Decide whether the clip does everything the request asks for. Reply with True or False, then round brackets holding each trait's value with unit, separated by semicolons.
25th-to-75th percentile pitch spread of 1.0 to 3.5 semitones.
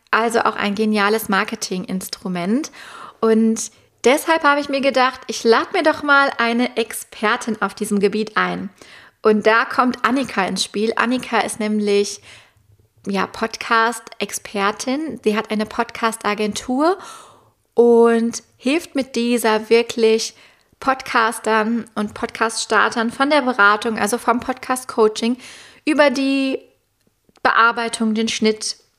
True (2.9 semitones)